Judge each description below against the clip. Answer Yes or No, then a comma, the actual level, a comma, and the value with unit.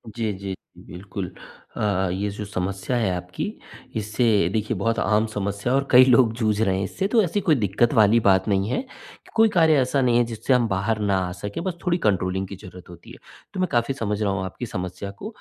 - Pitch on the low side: Yes, low, 105 Hz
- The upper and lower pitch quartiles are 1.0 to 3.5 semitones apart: No, average, 4.1 semitones